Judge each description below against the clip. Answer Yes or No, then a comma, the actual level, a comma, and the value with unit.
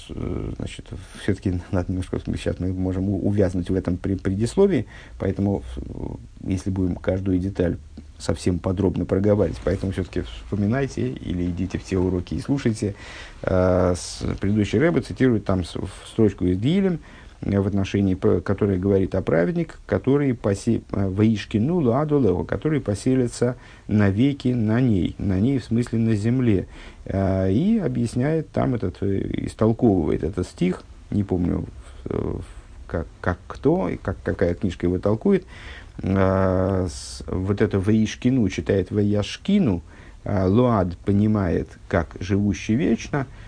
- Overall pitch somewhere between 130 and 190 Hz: No, low, 100 Hz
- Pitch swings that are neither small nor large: Yes, average, 3.9 semitones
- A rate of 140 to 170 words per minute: No, average, 120 wpm